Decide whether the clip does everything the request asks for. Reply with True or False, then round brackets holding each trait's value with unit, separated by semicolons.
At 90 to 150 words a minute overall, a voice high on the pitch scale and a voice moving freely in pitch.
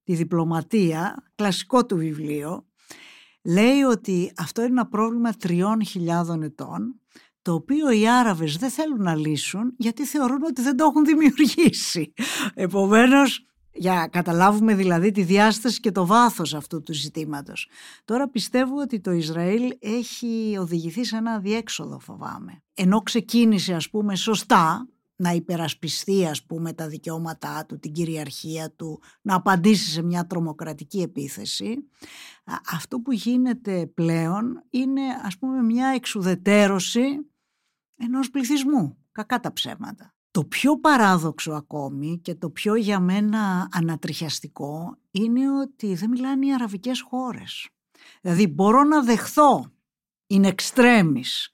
True (130 wpm; 205 Hz; 6.4 semitones)